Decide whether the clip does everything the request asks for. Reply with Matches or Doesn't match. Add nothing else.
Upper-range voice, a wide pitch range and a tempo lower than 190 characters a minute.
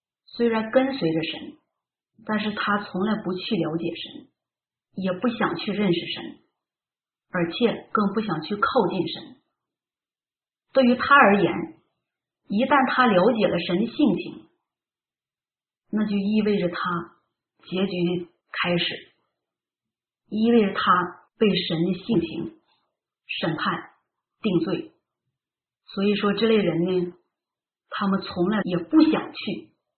Doesn't match